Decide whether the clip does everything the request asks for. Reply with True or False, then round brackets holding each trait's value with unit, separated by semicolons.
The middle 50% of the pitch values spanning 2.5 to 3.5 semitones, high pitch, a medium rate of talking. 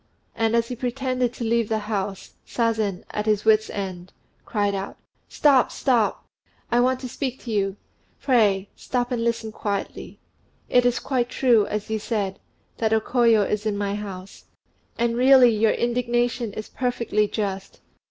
True (2.9 semitones; 225 Hz; 160 wpm)